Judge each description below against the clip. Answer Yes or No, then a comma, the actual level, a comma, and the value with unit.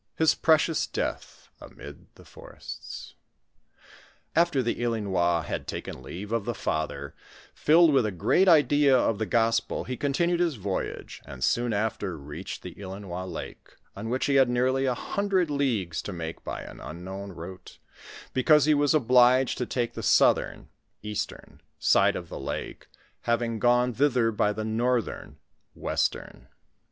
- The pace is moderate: Yes, average, 160 wpm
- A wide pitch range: Yes, wide, 5.8 semitones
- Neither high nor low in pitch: No, low, 115 Hz